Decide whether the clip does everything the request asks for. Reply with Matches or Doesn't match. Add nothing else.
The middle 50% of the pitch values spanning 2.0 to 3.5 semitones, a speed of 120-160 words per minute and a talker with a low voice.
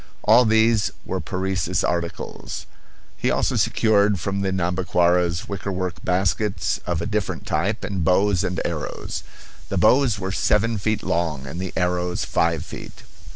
Matches